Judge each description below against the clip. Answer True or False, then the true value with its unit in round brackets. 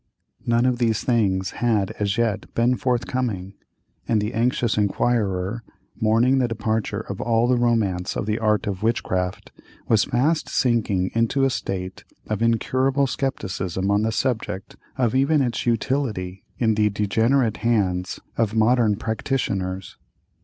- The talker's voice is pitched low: True (110 Hz)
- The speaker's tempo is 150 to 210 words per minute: False (140 wpm)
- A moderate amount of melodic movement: True (3.3 semitones)